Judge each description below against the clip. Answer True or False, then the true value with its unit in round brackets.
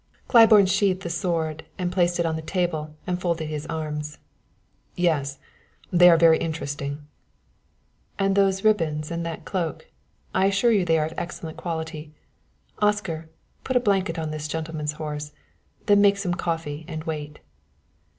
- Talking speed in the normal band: True (150 wpm)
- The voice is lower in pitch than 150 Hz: False (165 Hz)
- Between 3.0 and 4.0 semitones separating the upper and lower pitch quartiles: True (3.3 semitones)